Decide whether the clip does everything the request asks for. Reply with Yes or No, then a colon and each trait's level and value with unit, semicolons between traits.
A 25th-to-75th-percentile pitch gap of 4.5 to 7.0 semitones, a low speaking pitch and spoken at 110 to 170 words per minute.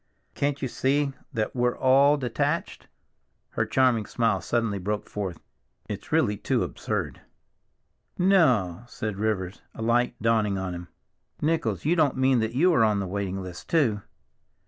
Yes: average, 4.8 semitones; low, 115 Hz; average, 150 wpm